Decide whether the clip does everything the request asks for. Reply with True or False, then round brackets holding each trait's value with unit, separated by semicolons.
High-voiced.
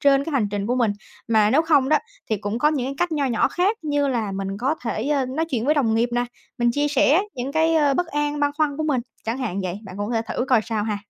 True (265 Hz)